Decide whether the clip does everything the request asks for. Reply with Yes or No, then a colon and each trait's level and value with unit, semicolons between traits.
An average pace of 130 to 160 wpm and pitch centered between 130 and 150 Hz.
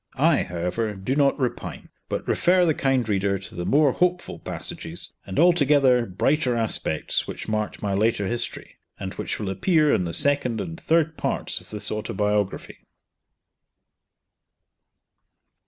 No: average, 140 wpm; low, 115 Hz